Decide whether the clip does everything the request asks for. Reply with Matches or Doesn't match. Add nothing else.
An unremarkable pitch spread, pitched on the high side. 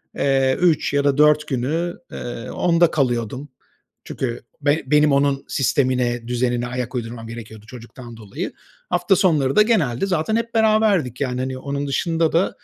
Doesn't match